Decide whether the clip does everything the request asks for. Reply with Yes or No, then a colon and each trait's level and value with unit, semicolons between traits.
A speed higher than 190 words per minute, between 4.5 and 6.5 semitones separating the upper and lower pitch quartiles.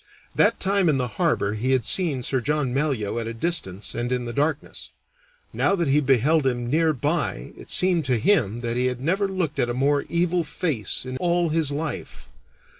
Yes: average, 200 wpm; average, 5.2 semitones